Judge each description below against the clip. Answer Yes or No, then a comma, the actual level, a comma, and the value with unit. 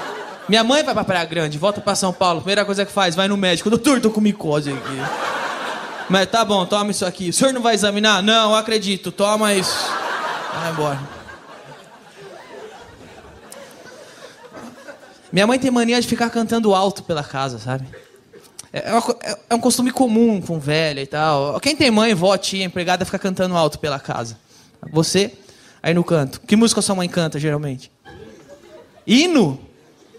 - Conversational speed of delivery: Yes, average, 165 wpm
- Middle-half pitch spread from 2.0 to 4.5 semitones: No, average, 5.2 semitones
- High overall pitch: Yes, high, 195 Hz